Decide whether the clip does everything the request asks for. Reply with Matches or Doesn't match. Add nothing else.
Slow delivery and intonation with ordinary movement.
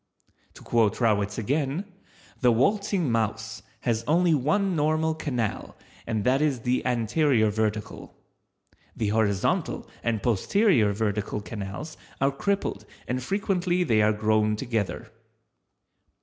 Doesn't match